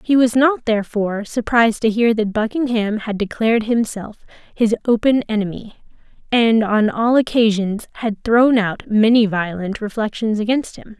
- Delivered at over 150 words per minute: No, average, 145 wpm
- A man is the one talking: No, female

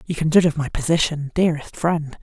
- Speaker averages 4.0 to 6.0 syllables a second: No, 6.3 syllables/s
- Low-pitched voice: No, medium, 155 Hz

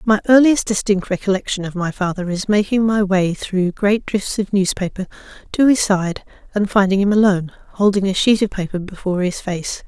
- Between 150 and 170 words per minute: No, average, 190 wpm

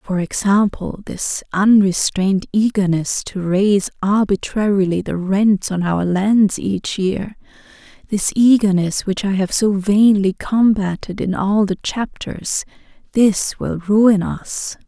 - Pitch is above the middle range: Yes, high, 200 Hz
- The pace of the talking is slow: Yes, slow, 125 wpm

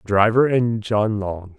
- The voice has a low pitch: Yes, low, 110 Hz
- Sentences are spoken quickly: No, average, 150 wpm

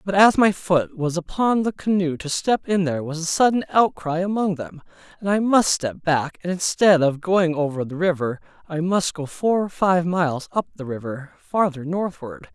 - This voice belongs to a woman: No, male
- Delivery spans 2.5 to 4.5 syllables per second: No, 4.8 syllables/s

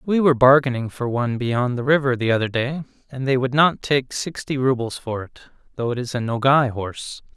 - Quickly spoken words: Yes, fast, 210 wpm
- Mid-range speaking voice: No, low, 130 Hz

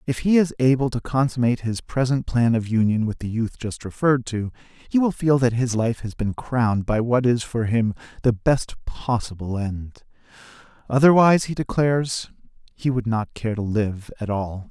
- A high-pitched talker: No, low, 120 Hz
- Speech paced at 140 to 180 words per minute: No, average, 190 wpm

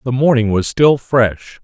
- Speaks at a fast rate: No, average, 185 wpm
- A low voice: Yes, low, 120 Hz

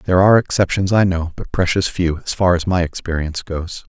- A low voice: Yes, very low, 90 Hz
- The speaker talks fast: Yes, fast, 215 wpm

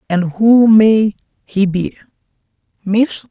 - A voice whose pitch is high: Yes, high, 205 Hz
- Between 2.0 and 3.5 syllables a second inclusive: Yes, 3.0 syllables/s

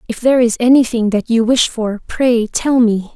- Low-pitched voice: No, high, 230 Hz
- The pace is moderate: No, fast, 210 wpm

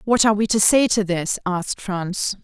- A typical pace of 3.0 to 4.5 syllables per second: No, 5.0 syllables/s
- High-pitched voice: Yes, high, 200 Hz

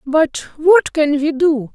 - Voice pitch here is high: Yes, very high, 305 Hz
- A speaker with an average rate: Yes, average, 170 wpm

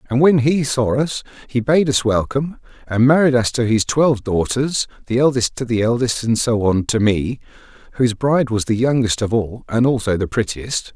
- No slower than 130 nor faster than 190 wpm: No, fast, 205 wpm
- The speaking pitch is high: No, low, 120 Hz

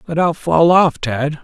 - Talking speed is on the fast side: Yes, fast, 210 wpm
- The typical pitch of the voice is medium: Yes, medium, 150 Hz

